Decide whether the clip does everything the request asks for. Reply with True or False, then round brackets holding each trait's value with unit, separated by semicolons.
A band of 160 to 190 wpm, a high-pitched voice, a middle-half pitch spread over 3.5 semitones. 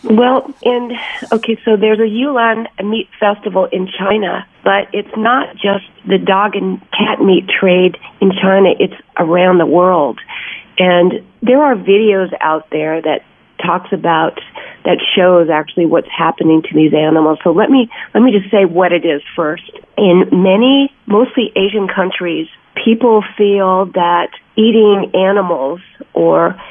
False (150 wpm; 195 Hz; 3.9 semitones)